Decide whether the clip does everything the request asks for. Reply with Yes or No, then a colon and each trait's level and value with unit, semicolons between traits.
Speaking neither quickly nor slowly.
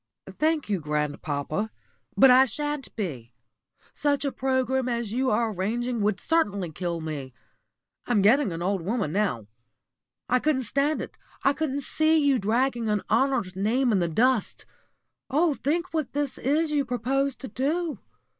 Yes: average, 155 wpm